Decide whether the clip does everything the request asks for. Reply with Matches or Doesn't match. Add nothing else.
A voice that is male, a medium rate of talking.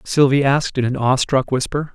Matches